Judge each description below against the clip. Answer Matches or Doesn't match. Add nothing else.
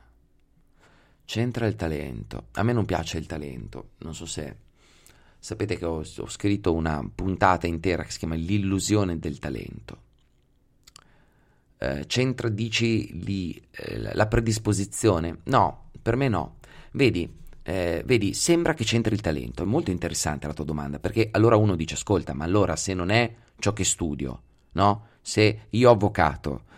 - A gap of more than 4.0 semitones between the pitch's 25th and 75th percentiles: Matches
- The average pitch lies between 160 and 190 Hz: Doesn't match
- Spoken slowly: Doesn't match